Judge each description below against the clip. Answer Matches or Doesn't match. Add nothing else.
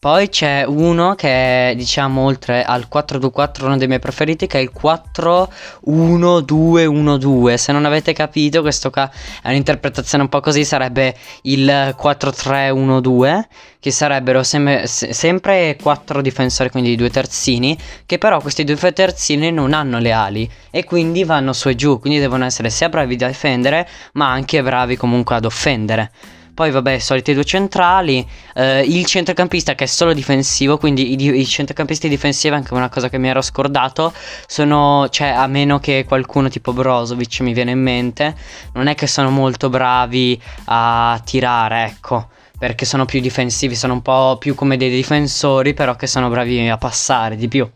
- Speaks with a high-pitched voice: Doesn't match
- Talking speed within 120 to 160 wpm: Doesn't match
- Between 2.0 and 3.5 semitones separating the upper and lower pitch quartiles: Matches